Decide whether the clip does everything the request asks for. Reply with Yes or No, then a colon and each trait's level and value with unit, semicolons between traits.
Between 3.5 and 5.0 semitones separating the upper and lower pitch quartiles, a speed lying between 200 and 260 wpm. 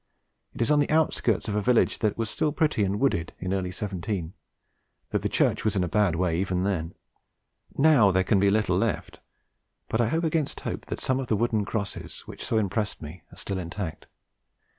Yes: average, 4.2 semitones; fast, 205 wpm